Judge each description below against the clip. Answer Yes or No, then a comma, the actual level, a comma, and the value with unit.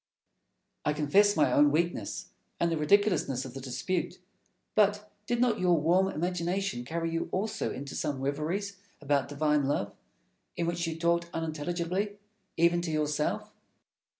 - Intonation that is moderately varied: Yes, average, 3.9 semitones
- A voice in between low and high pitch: Yes, medium, 170 Hz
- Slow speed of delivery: No, average, 150 wpm